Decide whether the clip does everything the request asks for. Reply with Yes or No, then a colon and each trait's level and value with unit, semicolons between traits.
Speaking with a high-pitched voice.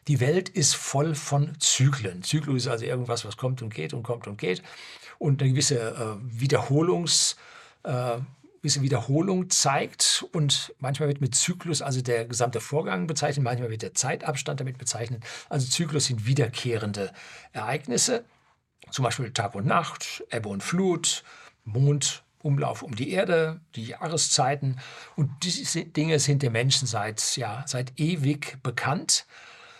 No: low, 135 Hz